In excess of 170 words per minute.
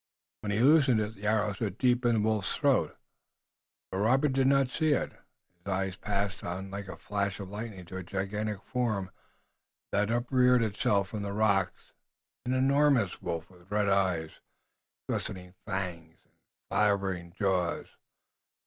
No: average, 155 wpm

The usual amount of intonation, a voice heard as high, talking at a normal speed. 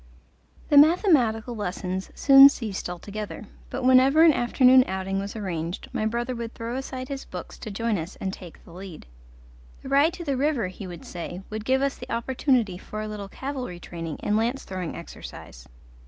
No: wide, 5.8 semitones; high, 220 Hz; average, 185 wpm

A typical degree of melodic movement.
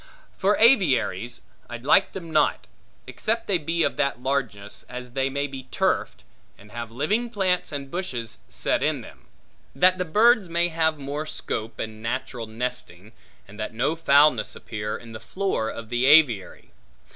No: wide, 6.6 semitones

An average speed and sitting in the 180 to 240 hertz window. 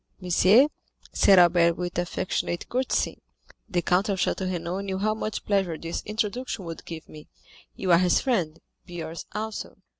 Yes: average, 160 wpm; medium, 185 Hz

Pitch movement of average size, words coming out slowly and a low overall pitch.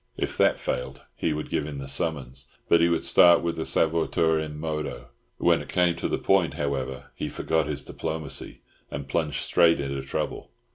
No: average, 3.0 semitones; average, 190 wpm; very low, 75 Hz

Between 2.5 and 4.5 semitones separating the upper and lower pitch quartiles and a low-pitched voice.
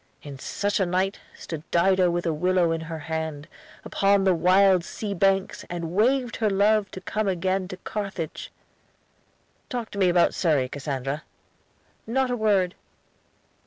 No: average, 3.3 semitones; medium, 185 Hz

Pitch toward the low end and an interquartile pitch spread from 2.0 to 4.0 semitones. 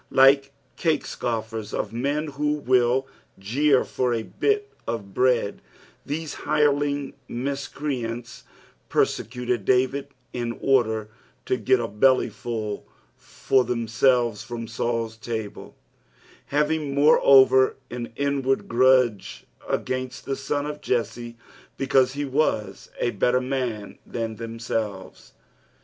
Yes: low, 125 Hz; average, 3.2 semitones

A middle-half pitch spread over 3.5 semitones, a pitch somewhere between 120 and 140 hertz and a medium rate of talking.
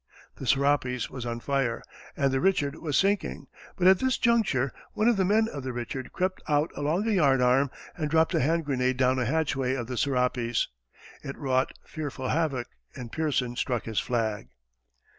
Yes: average, 4.1 semitones; low, 135 Hz; average, 180 wpm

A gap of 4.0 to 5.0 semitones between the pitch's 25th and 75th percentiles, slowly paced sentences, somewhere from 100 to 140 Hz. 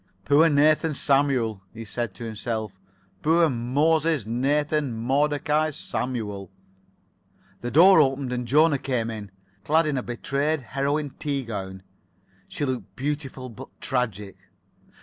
Yes: average, 4.4 semitones; slow, 125 wpm; low, 135 Hz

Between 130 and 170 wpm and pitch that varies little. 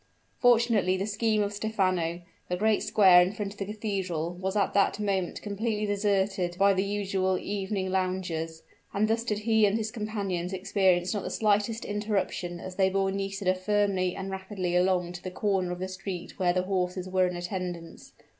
No: average, 185 wpm; narrow, 2.1 semitones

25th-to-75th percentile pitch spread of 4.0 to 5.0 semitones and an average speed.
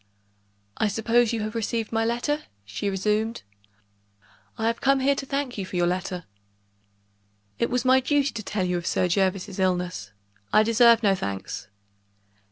Yes: average, 4.4 semitones; average, 165 wpm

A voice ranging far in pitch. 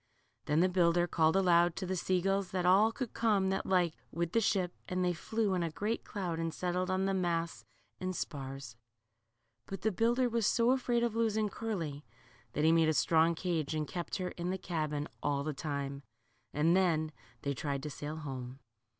No: average, 3.7 semitones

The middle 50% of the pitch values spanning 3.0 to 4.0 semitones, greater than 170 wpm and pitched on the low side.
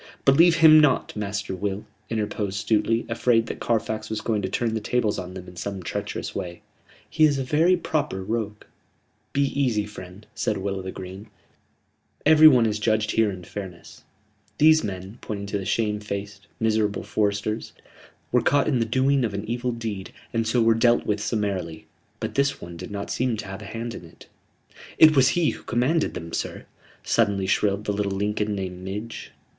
Yes: average, 3.3 semitones; average, 185 wpm; low, 105 Hz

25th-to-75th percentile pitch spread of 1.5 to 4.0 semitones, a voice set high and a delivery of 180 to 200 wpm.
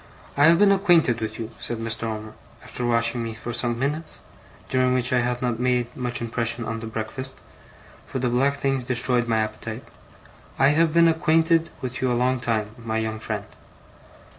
No: average, 2.8 semitones; low, 125 Hz; average, 190 wpm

